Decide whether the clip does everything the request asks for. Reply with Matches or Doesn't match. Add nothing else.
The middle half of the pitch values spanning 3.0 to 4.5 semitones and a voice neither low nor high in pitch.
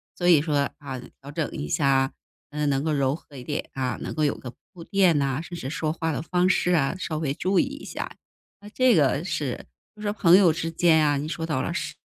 Matches